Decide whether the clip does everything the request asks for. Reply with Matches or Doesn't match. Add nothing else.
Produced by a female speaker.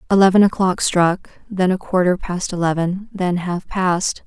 Matches